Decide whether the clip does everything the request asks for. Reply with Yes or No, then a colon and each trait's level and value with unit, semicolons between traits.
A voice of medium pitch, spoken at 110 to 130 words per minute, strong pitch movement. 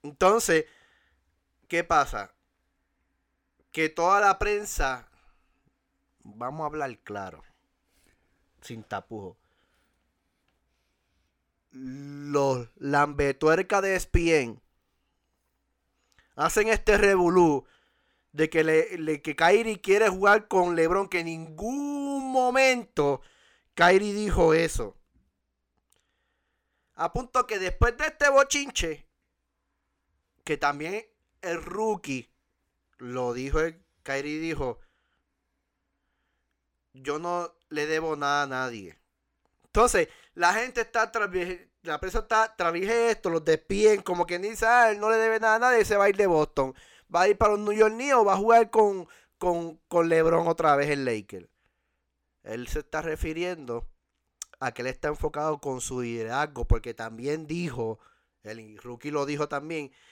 Yes: medium, 160 Hz; slow, 125 wpm; wide, 8.8 semitones